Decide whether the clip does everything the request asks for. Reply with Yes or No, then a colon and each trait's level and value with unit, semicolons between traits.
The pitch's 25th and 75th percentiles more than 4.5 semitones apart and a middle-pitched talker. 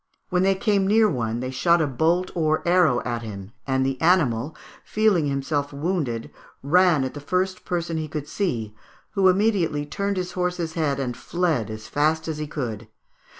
Yes: wide, 5.4 semitones; medium, 155 Hz